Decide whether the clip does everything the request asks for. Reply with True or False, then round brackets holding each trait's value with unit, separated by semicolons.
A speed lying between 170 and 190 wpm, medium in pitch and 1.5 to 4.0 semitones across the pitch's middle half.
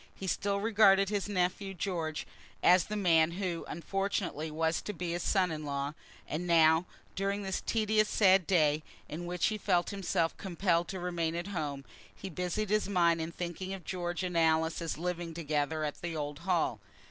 True (180 wpm; 175 Hz; 3.1 semitones)